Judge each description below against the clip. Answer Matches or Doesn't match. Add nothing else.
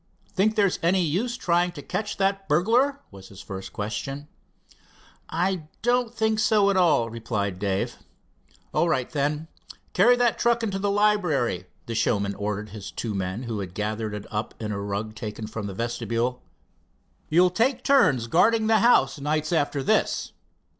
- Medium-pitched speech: Matches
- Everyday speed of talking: Matches